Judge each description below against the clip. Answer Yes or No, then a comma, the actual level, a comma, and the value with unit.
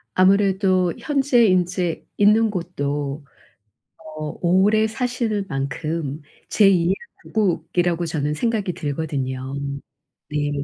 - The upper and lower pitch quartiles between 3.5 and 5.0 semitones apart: No, wide, 5.5 semitones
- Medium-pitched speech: Yes, medium, 180 Hz